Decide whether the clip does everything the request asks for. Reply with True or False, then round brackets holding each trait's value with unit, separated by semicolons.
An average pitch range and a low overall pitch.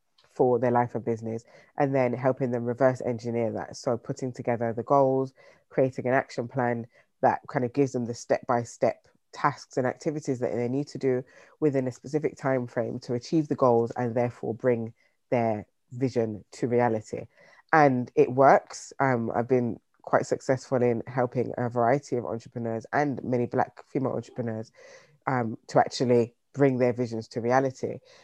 False (2.0 semitones; 125 Hz)